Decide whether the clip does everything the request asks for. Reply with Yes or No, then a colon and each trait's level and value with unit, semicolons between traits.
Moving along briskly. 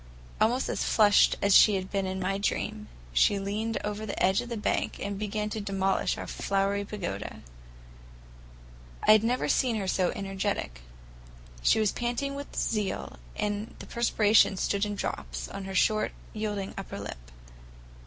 No: average, 165 wpm